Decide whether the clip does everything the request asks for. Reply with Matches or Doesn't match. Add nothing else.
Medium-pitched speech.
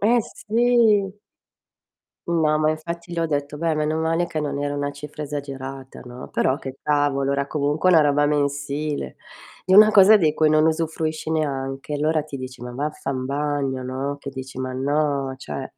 Matches